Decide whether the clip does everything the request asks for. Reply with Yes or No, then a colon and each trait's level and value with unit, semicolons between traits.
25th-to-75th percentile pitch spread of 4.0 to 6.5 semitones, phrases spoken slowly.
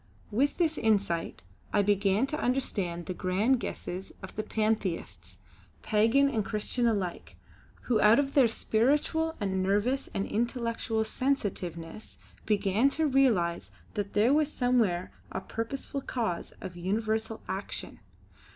Yes: average, 4.7 semitones; slow, 130 wpm